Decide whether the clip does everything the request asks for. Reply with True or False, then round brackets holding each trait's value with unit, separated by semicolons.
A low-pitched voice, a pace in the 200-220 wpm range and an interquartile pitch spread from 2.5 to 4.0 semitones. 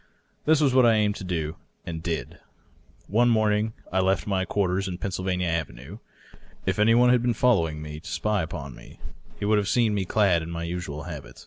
False (95 Hz; 205 wpm; 4.5 semitones)